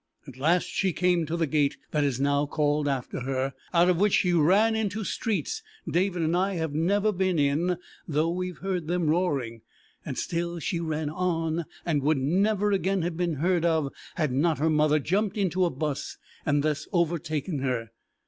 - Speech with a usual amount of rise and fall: Yes, average, 3.6 semitones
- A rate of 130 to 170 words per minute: No, average, 190 wpm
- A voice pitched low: No, medium, 165 Hz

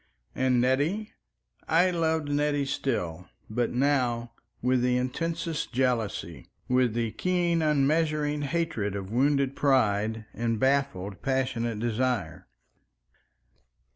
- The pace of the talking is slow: Yes, slow, 105 wpm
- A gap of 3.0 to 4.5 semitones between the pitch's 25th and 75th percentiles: Yes, average, 4.2 semitones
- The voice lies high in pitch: No, low, 130 Hz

